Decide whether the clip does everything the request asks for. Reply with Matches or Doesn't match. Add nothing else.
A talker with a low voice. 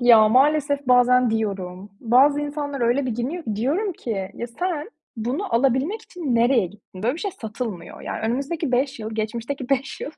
Doesn't match